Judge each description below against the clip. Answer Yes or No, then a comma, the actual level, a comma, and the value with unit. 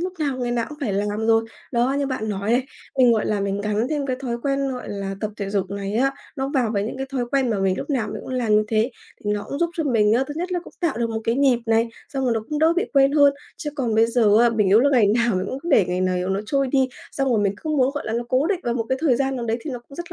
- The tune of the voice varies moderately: Yes, average, 4.3 semitones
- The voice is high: Yes, high, 240 Hz